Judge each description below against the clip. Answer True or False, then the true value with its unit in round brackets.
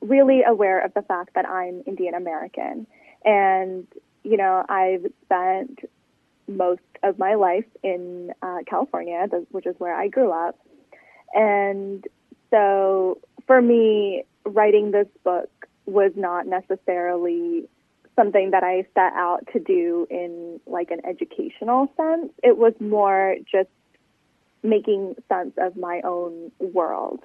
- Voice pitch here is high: True (195 Hz)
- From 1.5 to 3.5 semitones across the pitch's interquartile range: False (4.3 semitones)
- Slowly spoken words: True (130 wpm)